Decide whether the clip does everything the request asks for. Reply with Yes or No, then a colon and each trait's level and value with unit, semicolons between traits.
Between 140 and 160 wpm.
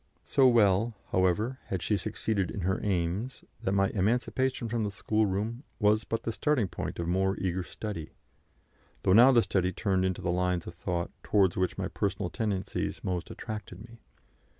No: average, 175 wpm